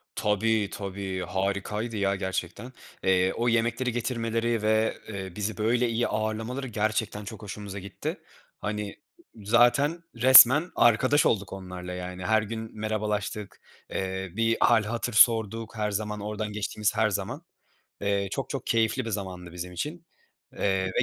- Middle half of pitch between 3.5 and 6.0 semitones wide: No, average, 2.7 semitones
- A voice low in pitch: Yes, low, 110 Hz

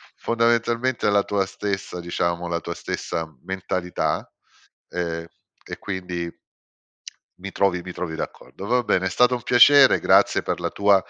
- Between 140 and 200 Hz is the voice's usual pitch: No, very low, 95 Hz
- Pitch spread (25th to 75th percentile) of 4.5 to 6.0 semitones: Yes, average, 4.8 semitones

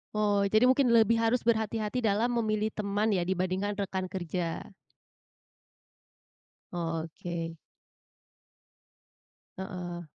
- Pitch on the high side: Yes, high, 200 Hz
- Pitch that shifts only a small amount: No, average, 3.4 semitones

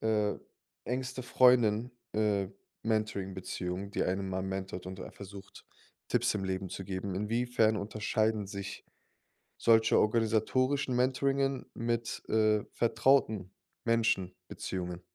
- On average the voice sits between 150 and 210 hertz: No, low, 105 Hz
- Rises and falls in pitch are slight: No, average, 3.4 semitones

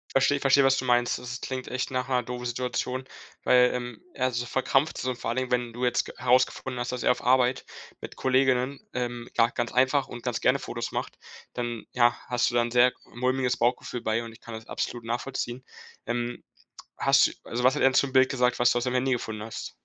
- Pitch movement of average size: No, narrow, 1.2 semitones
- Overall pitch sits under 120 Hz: No, low, 125 Hz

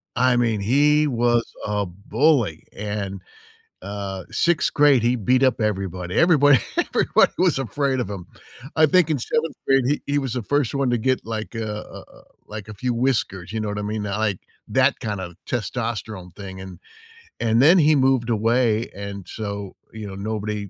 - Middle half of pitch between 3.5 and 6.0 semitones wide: Yes, average, 4.6 semitones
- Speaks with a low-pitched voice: Yes, low, 115 Hz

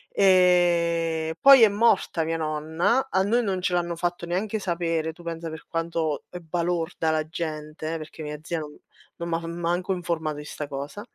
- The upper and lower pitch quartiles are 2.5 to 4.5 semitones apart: No, narrow, 1.9 semitones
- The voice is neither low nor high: Yes, medium, 170 Hz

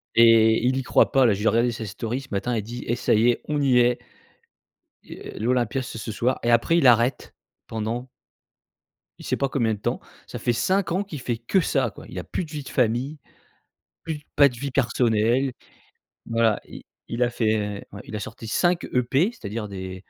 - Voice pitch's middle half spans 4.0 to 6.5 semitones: No, average, 3.2 semitones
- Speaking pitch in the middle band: No, low, 120 Hz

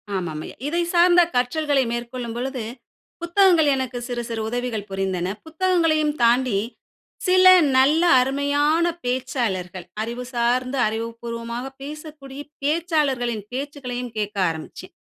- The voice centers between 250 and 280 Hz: Yes, very high, 255 Hz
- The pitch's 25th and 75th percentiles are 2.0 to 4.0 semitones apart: No, average, 4.4 semitones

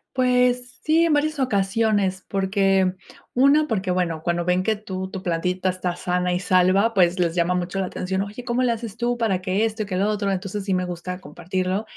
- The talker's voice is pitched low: No, high, 195 Hz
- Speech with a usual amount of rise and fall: Yes, average, 3.7 semitones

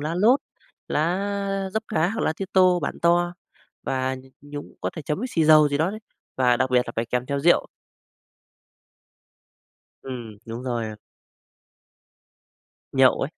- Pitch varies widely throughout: Yes, wide, 6.0 semitones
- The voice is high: No, medium, 150 Hz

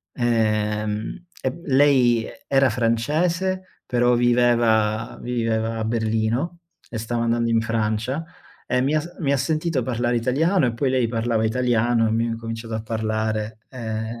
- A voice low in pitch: Yes, low, 120 Hz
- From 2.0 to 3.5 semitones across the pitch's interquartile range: Yes, average, 2.7 semitones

